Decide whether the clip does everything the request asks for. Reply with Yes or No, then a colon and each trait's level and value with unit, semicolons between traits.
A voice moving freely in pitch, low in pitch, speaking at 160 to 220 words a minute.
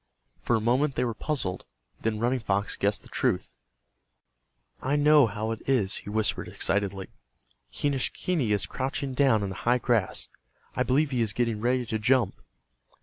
No: average, 3.9 semitones; low, 120 Hz; average, 165 wpm